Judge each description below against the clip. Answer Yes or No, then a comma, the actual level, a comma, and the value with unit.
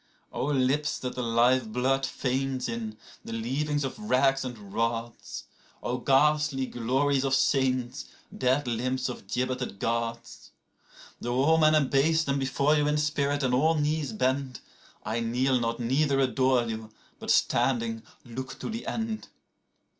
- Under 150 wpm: Yes, average, 140 wpm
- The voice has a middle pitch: No, low, 130 Hz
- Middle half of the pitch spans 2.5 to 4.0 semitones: Yes, average, 2.9 semitones